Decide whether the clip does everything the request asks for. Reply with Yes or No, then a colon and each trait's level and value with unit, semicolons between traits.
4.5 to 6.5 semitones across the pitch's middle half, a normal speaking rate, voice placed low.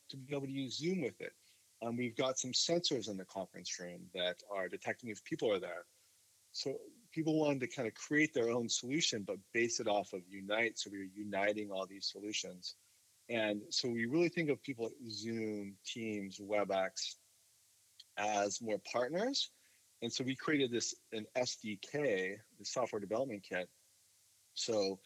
Yes: average, 5.1 semitones; average, 175 wpm; low, 115 Hz